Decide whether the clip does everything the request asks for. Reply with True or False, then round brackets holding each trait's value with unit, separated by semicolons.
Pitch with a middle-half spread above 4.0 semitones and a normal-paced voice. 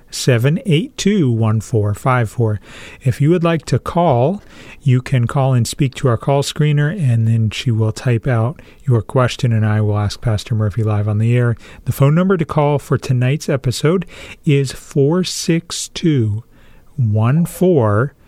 True (4.7 semitones; 175 wpm)